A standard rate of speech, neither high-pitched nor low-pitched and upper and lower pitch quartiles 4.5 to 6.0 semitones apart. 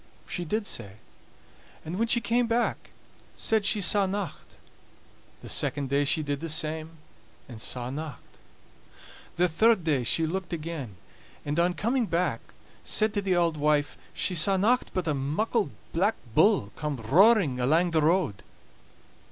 Yes: average, 155 wpm; medium, 170 Hz; wide, 5.4 semitones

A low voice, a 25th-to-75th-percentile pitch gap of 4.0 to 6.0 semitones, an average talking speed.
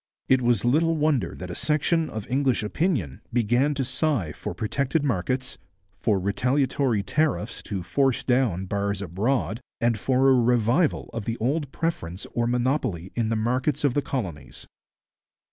Yes: low, 125 Hz; average, 5.0 semitones; average, 155 wpm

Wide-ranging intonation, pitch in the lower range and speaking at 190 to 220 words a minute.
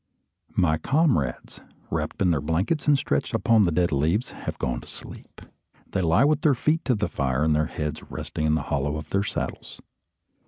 Yes: wide, 7.2 semitones; very low, 85 Hz; average, 195 wpm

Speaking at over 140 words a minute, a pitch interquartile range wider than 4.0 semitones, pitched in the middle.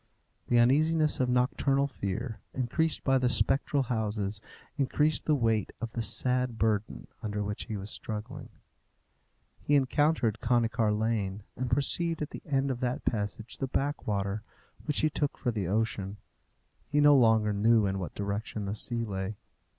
No: average, 160 wpm; average, 4.4 semitones; low, 115 Hz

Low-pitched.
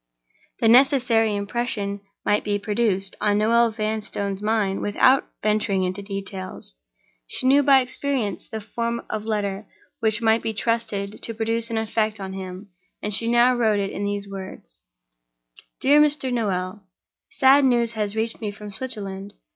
No: high, 215 Hz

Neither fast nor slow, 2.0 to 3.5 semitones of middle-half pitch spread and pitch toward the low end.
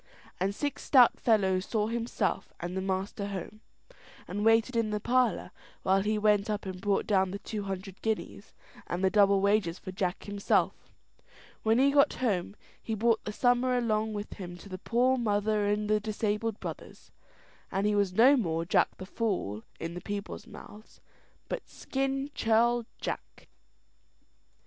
No: average, 165 wpm; average, 2.8 semitones; high, 210 Hz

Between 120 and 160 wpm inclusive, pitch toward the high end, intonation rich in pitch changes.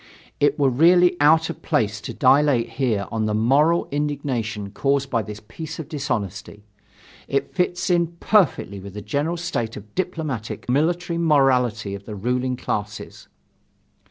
No: average, 155 wpm; low, 135 Hz; wide, 6.6 semitones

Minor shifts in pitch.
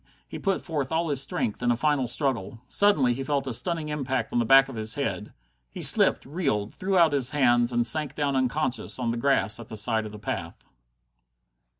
No: average, 4.0 semitones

